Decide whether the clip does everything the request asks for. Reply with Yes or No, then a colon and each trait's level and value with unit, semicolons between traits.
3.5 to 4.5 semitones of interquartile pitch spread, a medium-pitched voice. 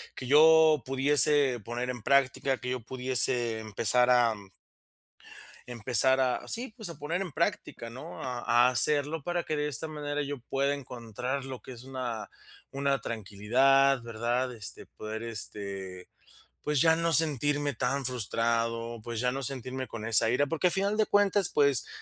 No: average, 3.8 semitones; low, 130 Hz